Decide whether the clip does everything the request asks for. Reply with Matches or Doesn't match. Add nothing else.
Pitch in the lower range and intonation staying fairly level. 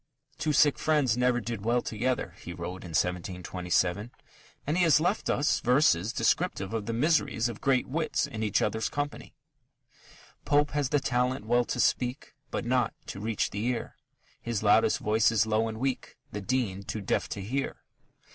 Doesn't match